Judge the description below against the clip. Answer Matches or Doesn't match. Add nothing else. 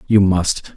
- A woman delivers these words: Doesn't match